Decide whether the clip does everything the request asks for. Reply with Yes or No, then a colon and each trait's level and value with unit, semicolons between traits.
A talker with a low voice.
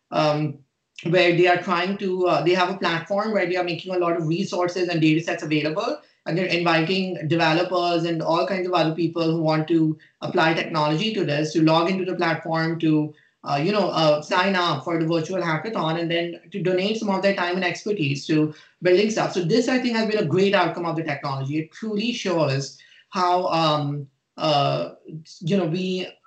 No: medium, 170 Hz